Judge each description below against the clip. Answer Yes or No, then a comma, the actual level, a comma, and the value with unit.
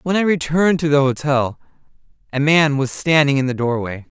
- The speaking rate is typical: Yes, average, 185 wpm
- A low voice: No, medium, 145 Hz